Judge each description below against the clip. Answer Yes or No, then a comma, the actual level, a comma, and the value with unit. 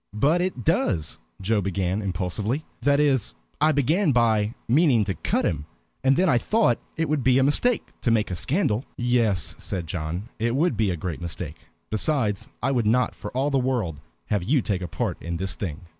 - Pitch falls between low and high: No, low, 115 Hz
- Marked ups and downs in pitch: Yes, wide, 6.5 semitones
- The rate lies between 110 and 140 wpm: No, average, 200 wpm